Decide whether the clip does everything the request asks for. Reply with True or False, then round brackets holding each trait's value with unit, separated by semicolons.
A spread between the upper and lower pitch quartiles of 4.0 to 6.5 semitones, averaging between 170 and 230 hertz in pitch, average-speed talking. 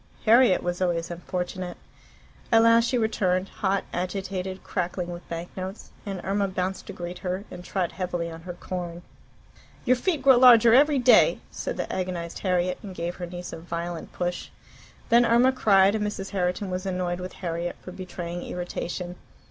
False (2.7 semitones; 185 Hz; 170 wpm)